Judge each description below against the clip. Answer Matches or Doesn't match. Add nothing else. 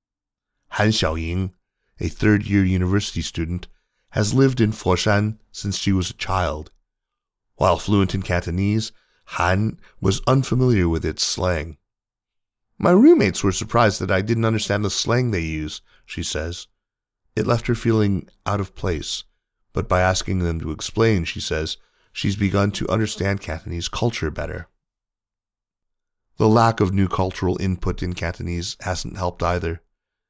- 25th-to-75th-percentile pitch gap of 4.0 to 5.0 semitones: Doesn't match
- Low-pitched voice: Matches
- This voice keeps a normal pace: Matches